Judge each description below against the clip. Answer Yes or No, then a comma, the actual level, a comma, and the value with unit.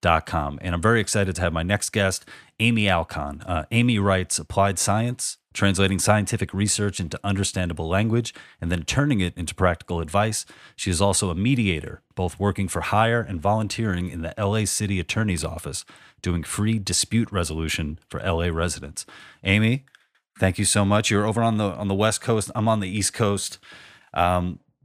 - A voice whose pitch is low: Yes, low, 100 Hz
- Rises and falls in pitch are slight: No, average, 3.3 semitones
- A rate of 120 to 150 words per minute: No, average, 180 wpm